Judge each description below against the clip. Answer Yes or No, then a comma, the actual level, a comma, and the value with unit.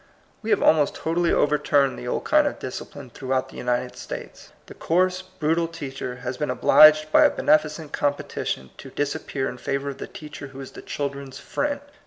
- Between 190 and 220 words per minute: Yes, average, 195 wpm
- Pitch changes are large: No, average, 3.8 semitones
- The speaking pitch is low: No, medium, 145 Hz